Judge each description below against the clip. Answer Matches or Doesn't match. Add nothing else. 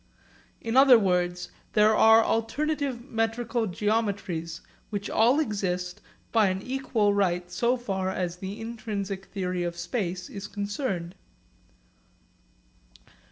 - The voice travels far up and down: Doesn't match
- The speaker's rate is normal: Doesn't match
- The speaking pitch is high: Matches